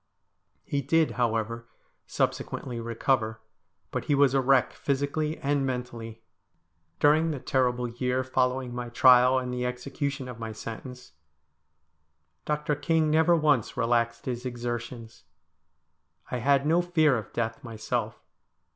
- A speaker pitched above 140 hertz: No, low, 125 Hz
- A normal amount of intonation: Yes, average, 3.2 semitones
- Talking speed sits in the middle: No, slow, 130 wpm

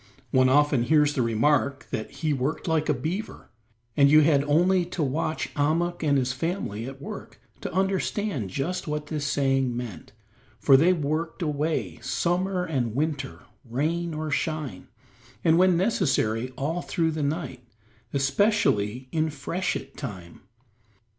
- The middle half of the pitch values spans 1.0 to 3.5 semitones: No, average, 3.9 semitones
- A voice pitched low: No, medium, 150 Hz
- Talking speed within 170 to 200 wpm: No, average, 145 wpm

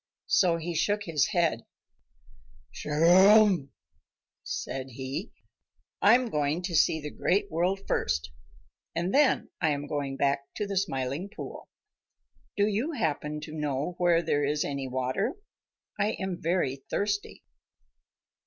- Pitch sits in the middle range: Yes, medium, 165 Hz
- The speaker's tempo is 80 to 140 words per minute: Yes, slow, 135 wpm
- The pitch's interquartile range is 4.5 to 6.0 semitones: Yes, wide, 5.6 semitones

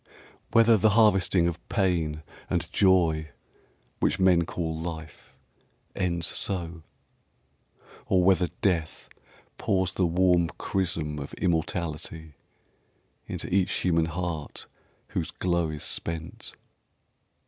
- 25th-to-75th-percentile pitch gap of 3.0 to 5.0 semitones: No, narrow, 2.4 semitones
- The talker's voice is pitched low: Yes, very low, 85 Hz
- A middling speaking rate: No, slow, 105 wpm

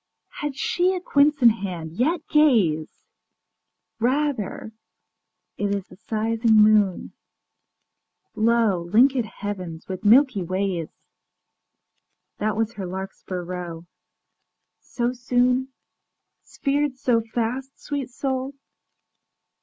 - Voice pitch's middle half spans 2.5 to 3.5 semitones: No, wide, 5.5 semitones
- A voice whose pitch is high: Yes, high, 225 Hz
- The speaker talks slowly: Yes, slow, 95 wpm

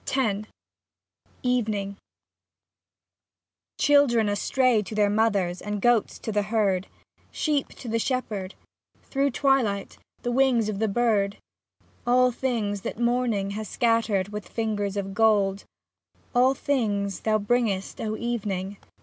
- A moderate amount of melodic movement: Yes, average, 3.3 semitones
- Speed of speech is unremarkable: No, slow, 130 wpm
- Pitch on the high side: Yes, high, 215 Hz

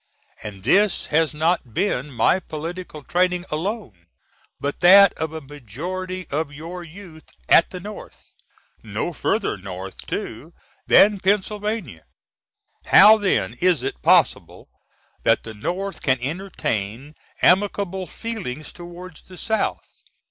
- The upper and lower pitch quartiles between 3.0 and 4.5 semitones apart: No, average, 5.2 semitones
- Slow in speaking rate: Yes, slow, 120 wpm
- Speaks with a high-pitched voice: No, medium, 175 Hz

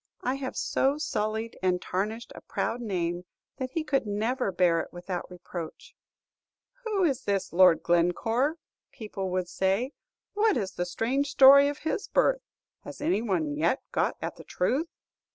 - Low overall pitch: No, high, 220 Hz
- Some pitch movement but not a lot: No, wide, 7.3 semitones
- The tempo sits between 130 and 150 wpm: No, average, 160 wpm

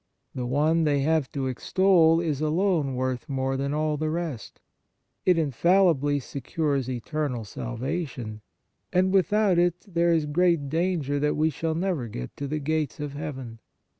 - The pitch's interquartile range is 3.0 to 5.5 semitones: Yes, average, 4.0 semitones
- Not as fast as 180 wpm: Yes, average, 160 wpm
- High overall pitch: No, medium, 150 Hz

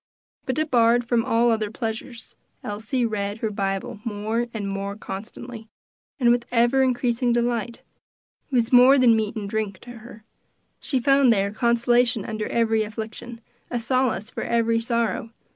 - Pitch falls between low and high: No, high, 230 Hz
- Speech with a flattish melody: Yes, narrow, 2.0 semitones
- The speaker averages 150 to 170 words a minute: Yes, average, 155 wpm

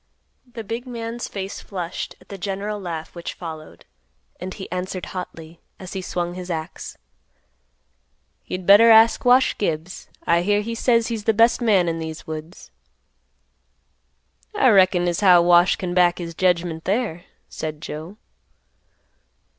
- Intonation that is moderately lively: Yes, average, 3.6 semitones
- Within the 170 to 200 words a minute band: No, average, 145 wpm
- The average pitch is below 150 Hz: No, medium, 185 Hz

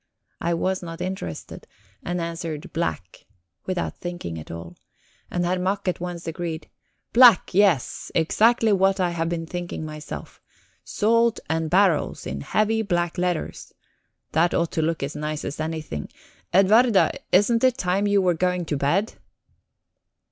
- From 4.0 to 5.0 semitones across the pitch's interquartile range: No, average, 3.2 semitones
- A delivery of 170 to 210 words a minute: No, average, 150 wpm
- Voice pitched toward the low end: No, medium, 175 Hz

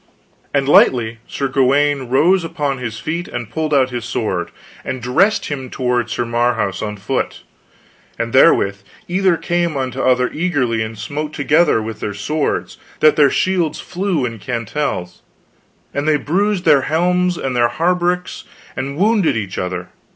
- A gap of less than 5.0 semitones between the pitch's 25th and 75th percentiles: No, wide, 5.5 semitones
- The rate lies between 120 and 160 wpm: Yes, average, 155 wpm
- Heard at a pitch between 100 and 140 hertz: Yes, low, 135 Hz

